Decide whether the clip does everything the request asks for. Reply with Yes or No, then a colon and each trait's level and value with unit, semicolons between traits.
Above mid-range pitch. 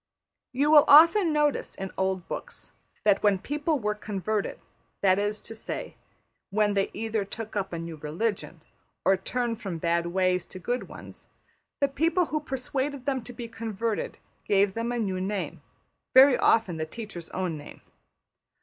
Yes: high, 215 Hz